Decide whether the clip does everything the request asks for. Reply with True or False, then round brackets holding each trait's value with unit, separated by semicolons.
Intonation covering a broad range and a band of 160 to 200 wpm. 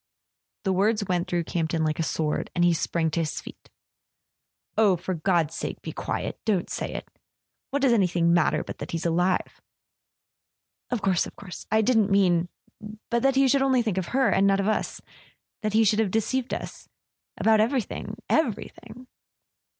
False (4.4 semitones; 180 wpm)